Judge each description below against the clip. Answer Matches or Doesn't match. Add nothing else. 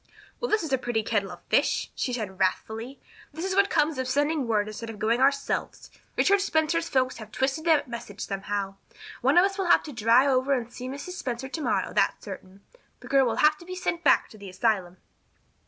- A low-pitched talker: Doesn't match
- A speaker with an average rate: Doesn't match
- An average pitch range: Doesn't match